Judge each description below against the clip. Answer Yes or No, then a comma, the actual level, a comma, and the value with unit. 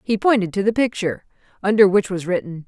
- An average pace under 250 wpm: Yes, average, 200 wpm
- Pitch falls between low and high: No, high, 195 Hz